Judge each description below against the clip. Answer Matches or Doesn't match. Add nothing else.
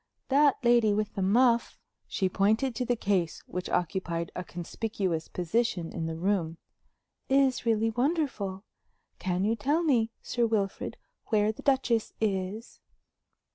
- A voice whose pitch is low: Doesn't match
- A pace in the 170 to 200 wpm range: Doesn't match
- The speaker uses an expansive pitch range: Doesn't match